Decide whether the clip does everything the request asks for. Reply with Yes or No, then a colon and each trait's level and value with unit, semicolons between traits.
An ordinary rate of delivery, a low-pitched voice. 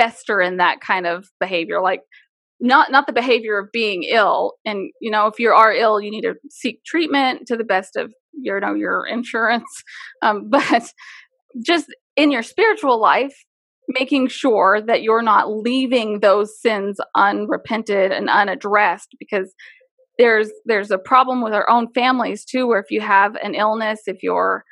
No: average, 170 wpm; high, 225 Hz